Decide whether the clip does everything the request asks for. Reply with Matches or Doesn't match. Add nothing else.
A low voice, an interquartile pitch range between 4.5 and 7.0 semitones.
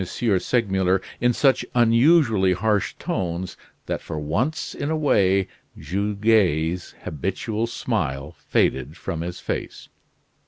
Matches